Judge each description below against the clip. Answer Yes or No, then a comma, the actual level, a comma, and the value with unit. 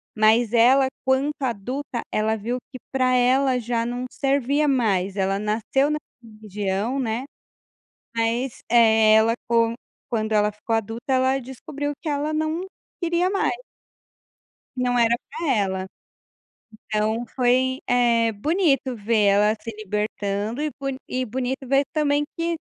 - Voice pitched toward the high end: Yes, high, 240 Hz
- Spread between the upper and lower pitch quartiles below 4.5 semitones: Yes, average, 3.8 semitones